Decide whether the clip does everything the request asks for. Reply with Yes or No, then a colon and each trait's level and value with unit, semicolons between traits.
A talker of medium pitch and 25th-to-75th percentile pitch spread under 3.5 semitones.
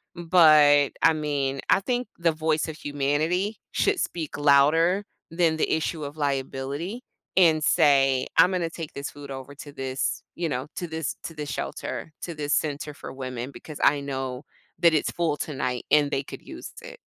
Yes: medium, 150 Hz; average, 2.8 semitones